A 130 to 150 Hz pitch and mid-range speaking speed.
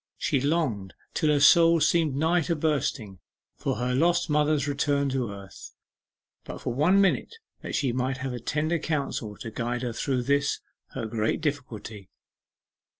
Yes: medium, 140 Hz; average, 155 wpm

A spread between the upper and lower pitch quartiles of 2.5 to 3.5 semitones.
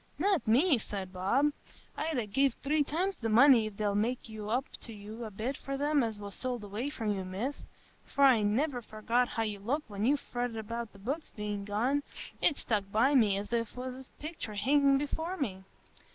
No: average, 4.9 semitones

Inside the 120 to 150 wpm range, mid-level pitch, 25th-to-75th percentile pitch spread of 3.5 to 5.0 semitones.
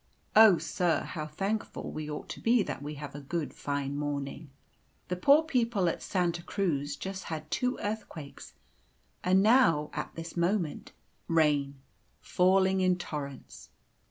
Yes: average, 145 wpm; medium, 170 Hz; average, 4.7 semitones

